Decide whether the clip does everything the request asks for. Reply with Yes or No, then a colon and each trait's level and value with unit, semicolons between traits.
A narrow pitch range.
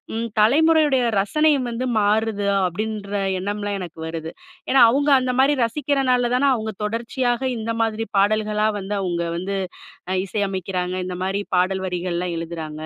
No: average, 4.6 semitones